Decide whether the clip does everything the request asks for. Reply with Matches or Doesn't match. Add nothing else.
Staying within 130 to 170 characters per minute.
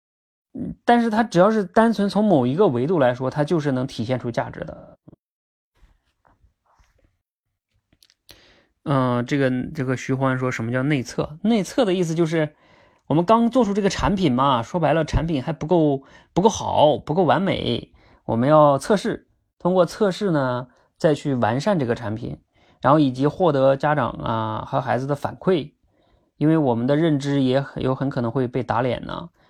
Doesn't match